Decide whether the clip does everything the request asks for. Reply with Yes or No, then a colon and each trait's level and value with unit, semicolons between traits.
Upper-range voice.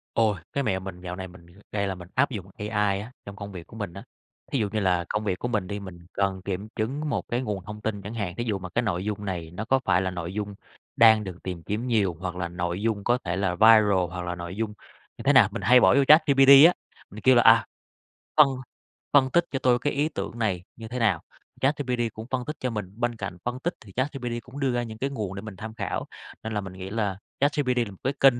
No: low, 105 Hz